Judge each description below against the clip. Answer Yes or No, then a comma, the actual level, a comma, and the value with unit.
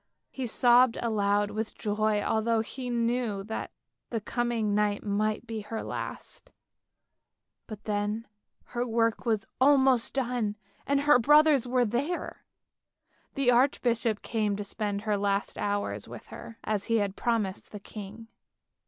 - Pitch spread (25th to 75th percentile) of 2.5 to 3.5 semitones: Yes, average, 2.8 semitones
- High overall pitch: Yes, high, 225 Hz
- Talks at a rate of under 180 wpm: Yes, average, 140 wpm